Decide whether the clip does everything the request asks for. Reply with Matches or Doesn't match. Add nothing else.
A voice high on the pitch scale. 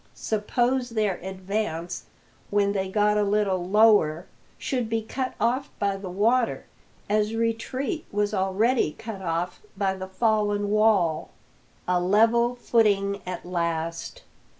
Matches